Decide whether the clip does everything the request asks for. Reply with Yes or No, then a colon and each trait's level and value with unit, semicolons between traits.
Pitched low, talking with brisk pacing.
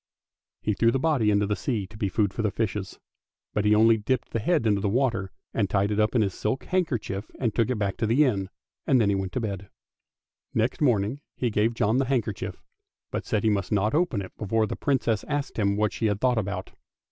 Yes: low, 110 Hz; fast, 235 wpm